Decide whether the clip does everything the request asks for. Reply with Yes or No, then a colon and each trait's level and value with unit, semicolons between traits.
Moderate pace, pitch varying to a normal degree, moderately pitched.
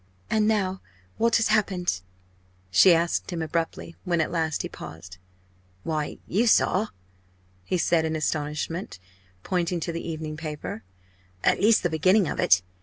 Yes: average, 150 wpm; average, 3.2 semitones; medium, 170 Hz